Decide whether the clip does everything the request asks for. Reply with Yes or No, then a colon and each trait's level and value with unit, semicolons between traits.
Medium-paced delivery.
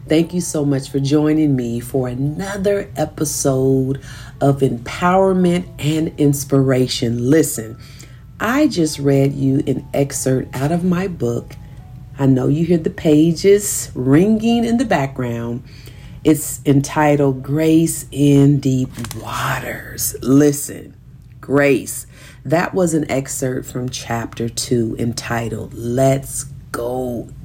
No: slow, 115 wpm